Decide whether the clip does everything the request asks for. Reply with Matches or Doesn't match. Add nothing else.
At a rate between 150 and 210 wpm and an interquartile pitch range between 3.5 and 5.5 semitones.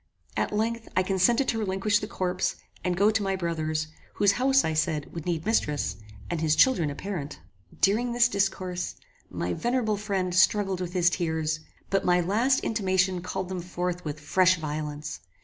Matches